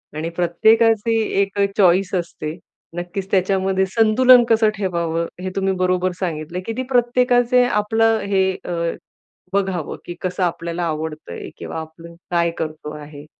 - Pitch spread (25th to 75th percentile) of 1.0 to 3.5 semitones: No, average, 4.3 semitones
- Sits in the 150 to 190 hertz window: Yes, medium, 185 Hz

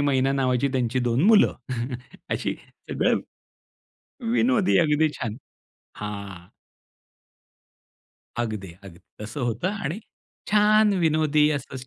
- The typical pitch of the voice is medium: No, low, 130 Hz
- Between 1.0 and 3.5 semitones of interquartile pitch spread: No, wide, 5.5 semitones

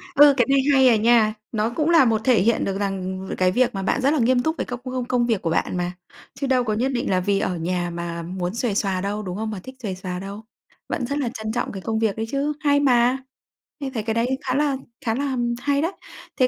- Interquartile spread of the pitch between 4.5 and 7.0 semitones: Yes, average, 5.1 semitones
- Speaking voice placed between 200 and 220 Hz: No, high, 230 Hz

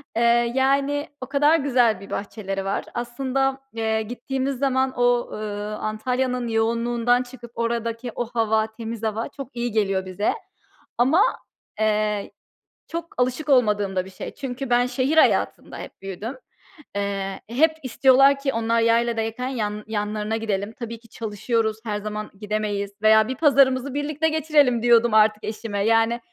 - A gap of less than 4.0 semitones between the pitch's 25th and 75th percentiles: Yes, average, 3.3 semitones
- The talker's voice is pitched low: No, high, 230 Hz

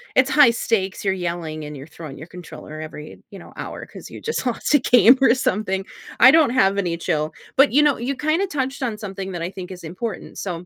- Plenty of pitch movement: Yes, wide, 7.1 semitones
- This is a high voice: Yes, high, 195 Hz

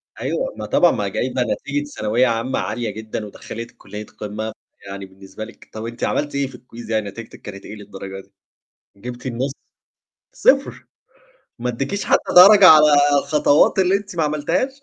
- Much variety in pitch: Yes, wide, 6.2 semitones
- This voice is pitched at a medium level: No, low, 120 Hz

